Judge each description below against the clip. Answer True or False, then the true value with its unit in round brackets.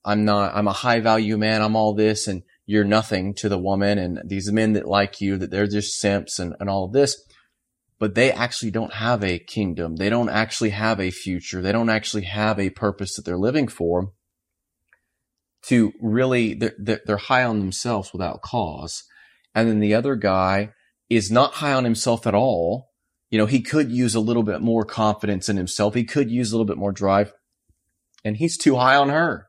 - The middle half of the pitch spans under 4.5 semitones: True (2.6 semitones)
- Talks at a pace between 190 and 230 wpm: True (205 wpm)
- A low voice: True (105 Hz)